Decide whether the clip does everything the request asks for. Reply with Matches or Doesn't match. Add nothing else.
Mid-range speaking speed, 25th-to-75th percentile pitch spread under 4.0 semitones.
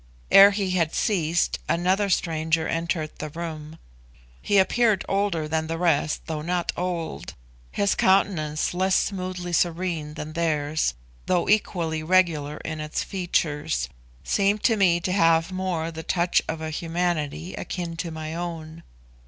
Matches